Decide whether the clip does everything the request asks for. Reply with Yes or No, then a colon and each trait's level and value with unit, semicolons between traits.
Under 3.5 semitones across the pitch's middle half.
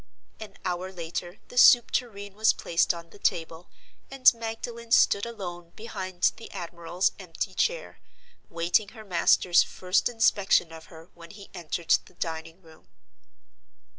No: average, 4.4 semitones